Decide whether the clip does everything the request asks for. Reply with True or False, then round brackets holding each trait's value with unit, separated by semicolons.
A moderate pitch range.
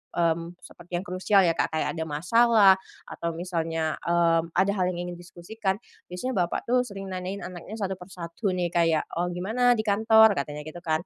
True (3.0 semitones)